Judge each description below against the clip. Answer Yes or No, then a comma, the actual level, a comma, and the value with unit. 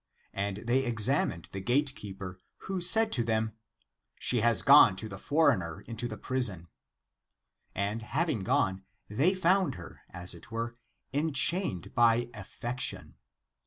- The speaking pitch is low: Yes, low, 115 Hz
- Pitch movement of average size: No, wide, 6.0 semitones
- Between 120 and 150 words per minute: Yes, average, 140 wpm